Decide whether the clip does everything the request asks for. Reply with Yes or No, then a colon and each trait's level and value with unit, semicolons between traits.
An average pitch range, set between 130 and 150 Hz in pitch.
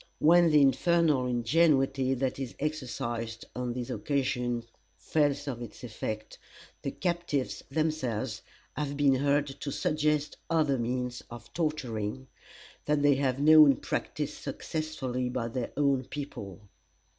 Yes: average, 3.6 semitones; low, 135 Hz